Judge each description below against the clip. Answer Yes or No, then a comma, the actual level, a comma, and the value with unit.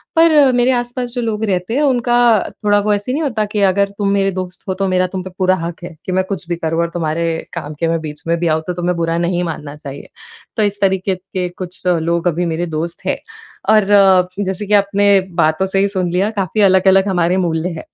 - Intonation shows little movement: No, average, 3.3 semitones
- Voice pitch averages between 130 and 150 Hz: No, medium, 185 Hz